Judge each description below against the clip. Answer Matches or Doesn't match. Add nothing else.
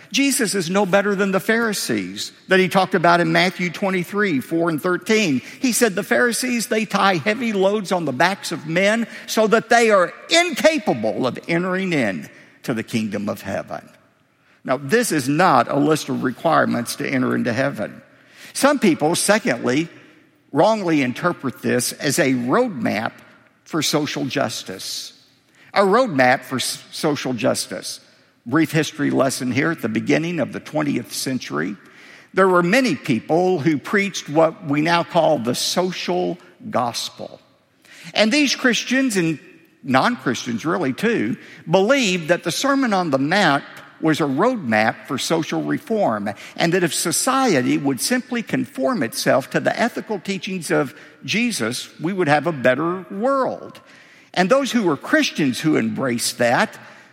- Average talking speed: Matches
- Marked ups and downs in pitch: Matches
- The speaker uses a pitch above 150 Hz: Matches